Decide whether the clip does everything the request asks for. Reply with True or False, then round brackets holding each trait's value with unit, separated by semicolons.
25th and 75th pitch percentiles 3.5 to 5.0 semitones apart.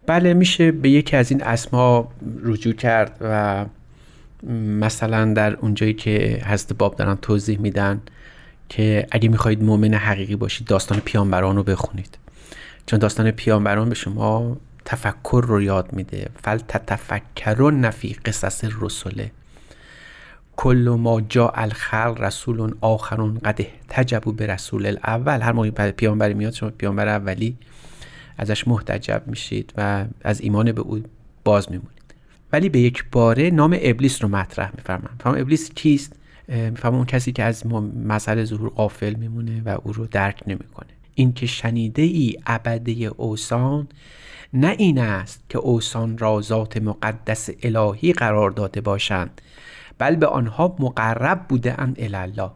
False (2.9 semitones)